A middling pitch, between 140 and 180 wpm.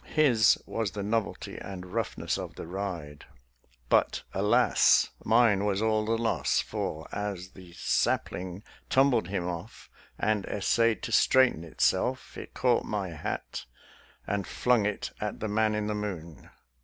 No: low, 105 Hz; average, 145 wpm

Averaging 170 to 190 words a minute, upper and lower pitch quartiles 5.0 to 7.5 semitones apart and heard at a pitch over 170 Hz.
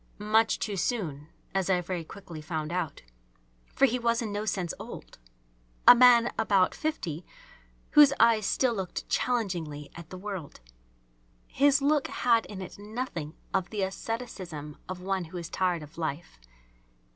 No: average, 155 wpm; wide, 5.4 semitones; high, 190 Hz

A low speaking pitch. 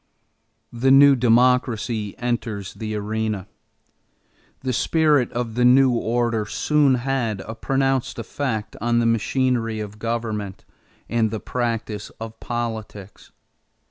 Yes: low, 115 Hz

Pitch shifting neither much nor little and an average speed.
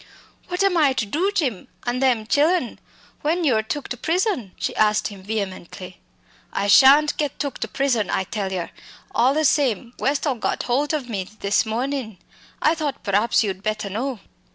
No: wide, 5.7 semitones; average, 175 wpm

